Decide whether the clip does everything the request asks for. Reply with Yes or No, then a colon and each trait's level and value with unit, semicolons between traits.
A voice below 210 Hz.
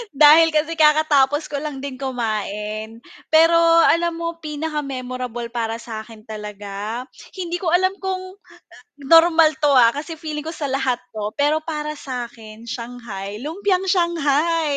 No: very high, 285 Hz